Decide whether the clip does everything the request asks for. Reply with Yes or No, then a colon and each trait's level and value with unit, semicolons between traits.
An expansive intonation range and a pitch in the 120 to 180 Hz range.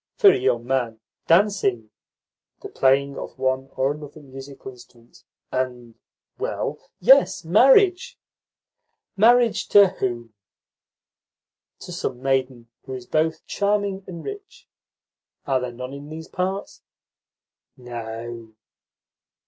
Yes: wide, 7.5 semitones; low, 135 Hz